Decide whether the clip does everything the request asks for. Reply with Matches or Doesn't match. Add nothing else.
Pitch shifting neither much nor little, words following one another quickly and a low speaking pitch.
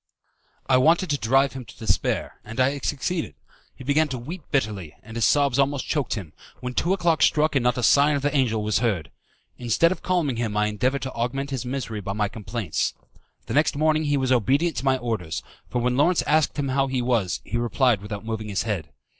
Matches